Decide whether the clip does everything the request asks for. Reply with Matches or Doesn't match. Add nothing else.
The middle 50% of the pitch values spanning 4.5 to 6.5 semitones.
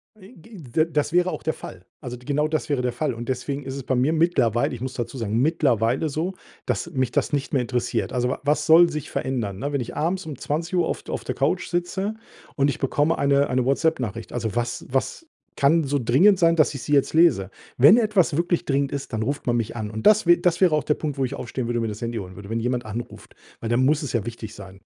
Matches